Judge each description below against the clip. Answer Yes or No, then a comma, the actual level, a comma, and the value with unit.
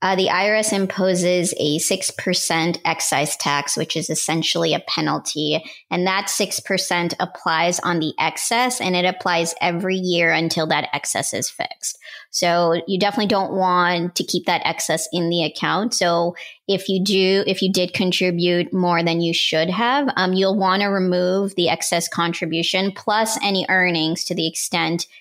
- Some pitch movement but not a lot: No, narrow, 2.3 semitones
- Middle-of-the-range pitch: Yes, medium, 180 Hz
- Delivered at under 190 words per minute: Yes, average, 165 wpm